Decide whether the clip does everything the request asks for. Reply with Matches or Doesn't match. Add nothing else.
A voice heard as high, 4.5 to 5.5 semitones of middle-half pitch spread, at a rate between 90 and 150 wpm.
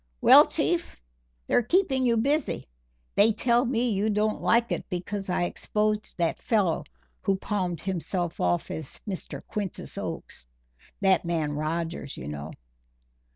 Matches